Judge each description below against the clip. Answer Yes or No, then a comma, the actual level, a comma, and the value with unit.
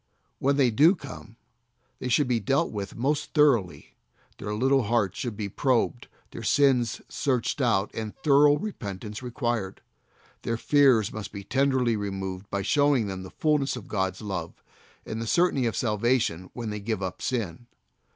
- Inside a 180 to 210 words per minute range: No, average, 160 wpm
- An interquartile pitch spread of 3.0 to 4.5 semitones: No, average, 5.0 semitones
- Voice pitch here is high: No, low, 115 Hz